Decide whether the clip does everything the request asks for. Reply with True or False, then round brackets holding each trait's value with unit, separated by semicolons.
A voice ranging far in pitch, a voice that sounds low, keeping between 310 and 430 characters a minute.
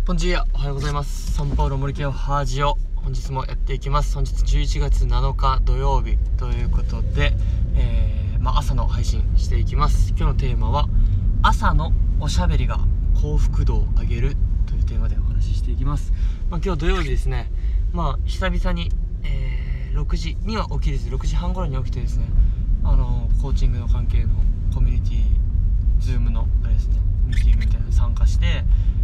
False (4.2 semitones; 90 Hz; 370 characters per minute)